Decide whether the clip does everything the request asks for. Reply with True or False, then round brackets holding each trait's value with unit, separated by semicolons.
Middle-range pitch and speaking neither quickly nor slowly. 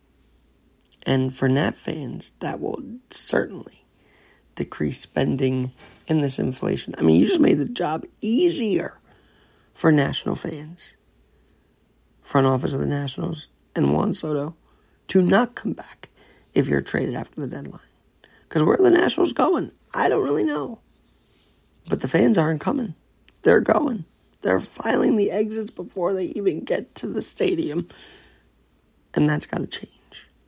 True (145 Hz; 145 wpm)